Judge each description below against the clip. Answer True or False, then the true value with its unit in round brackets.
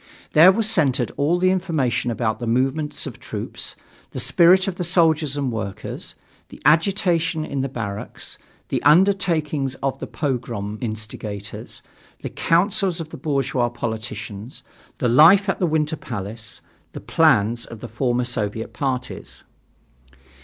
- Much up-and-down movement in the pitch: True (6.3 semitones)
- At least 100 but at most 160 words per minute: True (145 wpm)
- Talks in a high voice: False (135 Hz)